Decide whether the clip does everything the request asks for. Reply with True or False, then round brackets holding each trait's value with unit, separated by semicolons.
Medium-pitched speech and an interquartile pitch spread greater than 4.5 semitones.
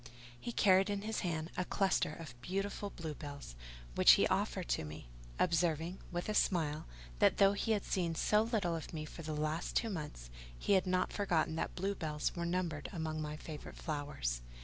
False (170 Hz; 4.0 semitones)